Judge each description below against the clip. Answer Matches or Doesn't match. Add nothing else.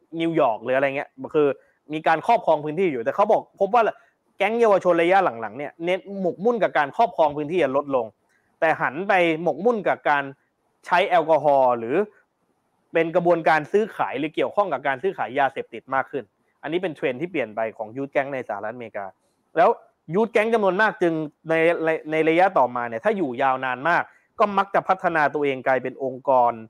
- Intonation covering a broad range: Matches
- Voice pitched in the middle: Matches